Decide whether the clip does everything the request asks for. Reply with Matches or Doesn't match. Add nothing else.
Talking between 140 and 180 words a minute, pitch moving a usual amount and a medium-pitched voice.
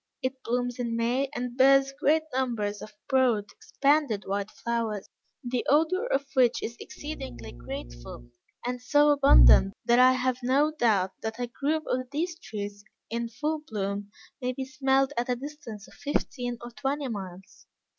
Doesn't match